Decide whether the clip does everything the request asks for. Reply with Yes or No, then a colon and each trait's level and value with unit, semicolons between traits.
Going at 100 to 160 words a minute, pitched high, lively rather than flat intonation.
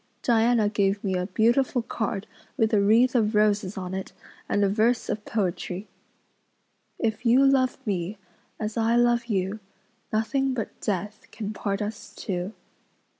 No: average, 150 wpm; high, 215 Hz; average, 2.8 semitones